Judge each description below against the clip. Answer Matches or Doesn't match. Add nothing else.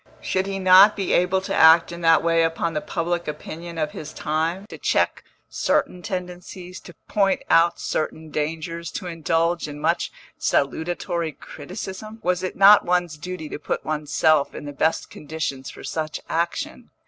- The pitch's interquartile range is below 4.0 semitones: Matches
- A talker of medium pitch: Matches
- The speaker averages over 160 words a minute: Matches